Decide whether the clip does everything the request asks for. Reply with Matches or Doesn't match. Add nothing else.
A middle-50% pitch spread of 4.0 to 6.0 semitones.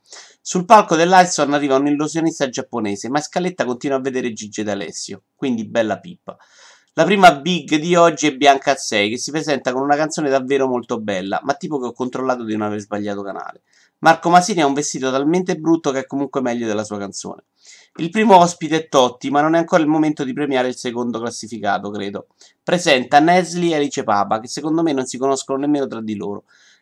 Matches